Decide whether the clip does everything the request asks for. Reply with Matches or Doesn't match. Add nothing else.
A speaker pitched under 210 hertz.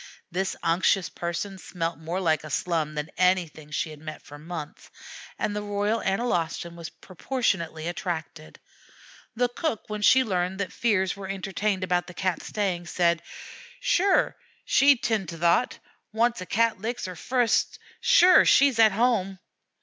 Matches